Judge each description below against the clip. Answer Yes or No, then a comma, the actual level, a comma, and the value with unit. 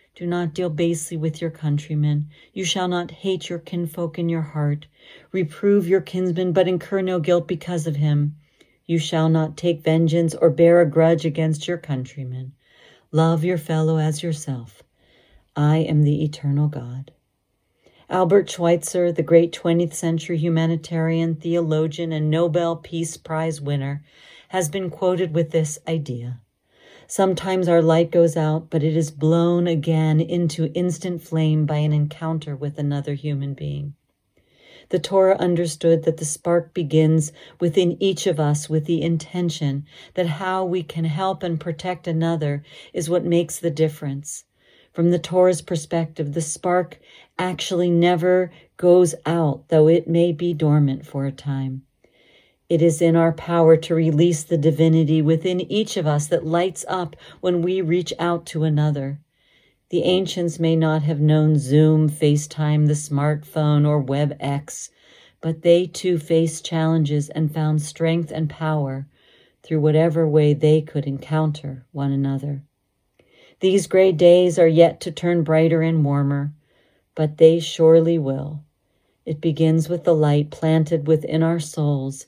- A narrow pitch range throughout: Yes, narrow, 2.2 semitones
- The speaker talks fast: No, average, 150 wpm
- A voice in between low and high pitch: Yes, medium, 160 Hz